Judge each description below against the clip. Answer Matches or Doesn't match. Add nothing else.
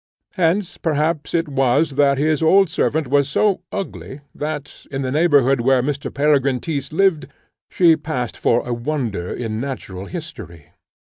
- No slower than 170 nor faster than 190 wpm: Doesn't match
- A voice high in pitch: Doesn't match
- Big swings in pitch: Doesn't match